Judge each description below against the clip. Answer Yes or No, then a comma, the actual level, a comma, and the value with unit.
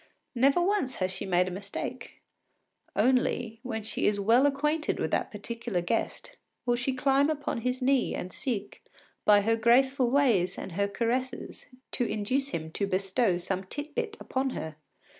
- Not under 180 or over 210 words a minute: No, average, 165 wpm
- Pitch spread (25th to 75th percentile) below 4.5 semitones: No, average, 5.2 semitones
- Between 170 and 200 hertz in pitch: No, high, 235 Hz